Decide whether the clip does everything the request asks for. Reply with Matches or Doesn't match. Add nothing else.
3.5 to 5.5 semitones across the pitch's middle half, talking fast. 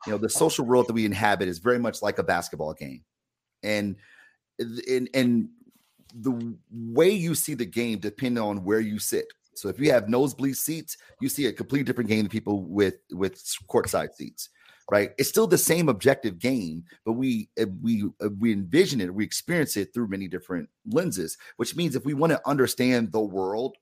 Doesn't match